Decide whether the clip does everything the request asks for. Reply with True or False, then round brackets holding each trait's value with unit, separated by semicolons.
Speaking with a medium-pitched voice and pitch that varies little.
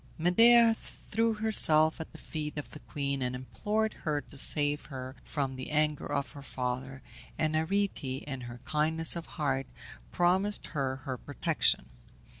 False (150 Hz; 4.4 semitones)